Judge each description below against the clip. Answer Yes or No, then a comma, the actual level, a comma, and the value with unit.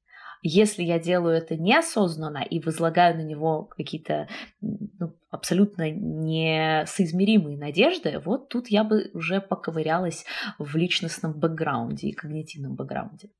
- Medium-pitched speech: Yes, medium, 170 Hz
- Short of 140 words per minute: Yes, average, 115 wpm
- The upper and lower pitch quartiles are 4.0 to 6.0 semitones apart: Yes, average, 4.4 semitones